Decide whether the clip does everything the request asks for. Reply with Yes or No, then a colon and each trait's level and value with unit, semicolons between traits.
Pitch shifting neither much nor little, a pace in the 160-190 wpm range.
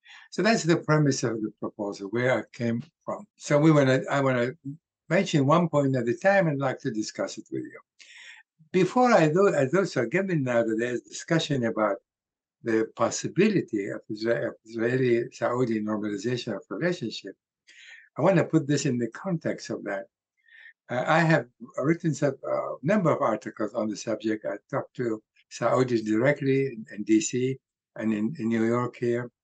No: wide, 5.8 semitones; average, 175 wpm